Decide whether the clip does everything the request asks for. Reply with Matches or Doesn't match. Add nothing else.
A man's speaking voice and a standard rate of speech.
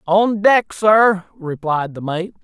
Matches